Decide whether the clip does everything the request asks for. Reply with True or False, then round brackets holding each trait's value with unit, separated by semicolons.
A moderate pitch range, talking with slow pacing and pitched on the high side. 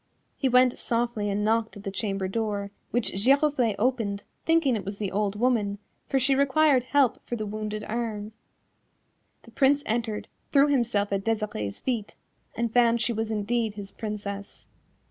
False (3.4 semitones; 165 wpm; 225 Hz)